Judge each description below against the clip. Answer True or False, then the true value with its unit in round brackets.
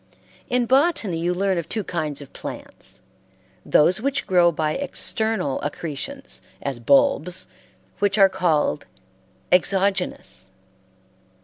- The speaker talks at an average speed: False (110 wpm)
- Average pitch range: False (5.8 semitones)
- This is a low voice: False (180 Hz)